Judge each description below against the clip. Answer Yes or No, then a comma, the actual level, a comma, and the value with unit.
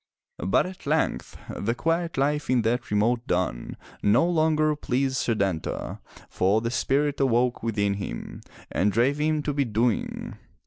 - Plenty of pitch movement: Yes, wide, 5.8 semitones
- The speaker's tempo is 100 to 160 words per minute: Yes, average, 145 wpm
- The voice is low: Yes, low, 125 Hz